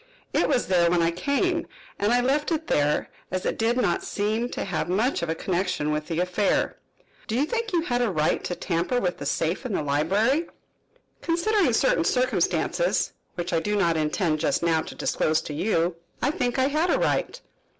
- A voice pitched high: Yes, high, 200 Hz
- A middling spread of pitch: No, wide, 7.6 semitones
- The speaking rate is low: No, average, 200 wpm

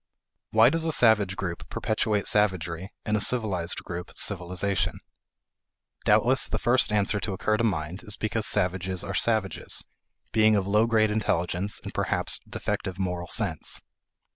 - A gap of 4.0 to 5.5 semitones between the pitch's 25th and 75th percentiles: No, average, 3.0 semitones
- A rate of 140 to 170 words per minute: Yes, average, 145 wpm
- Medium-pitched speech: No, low, 100 Hz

